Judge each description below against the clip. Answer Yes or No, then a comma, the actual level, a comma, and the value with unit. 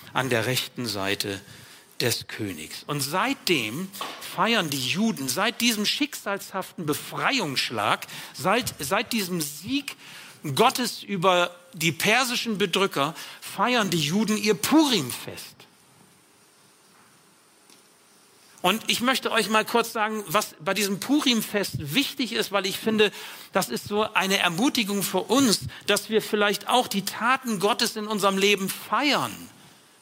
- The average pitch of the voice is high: Yes, high, 200 Hz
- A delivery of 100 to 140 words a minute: Yes, slow, 125 wpm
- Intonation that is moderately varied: Yes, average, 4.1 semitones